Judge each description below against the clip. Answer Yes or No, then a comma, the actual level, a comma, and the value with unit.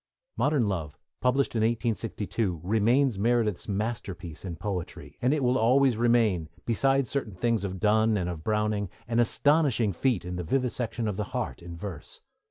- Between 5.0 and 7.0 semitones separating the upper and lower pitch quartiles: No, average, 4.2 semitones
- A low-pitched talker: Yes, low, 110 Hz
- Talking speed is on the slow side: No, average, 165 wpm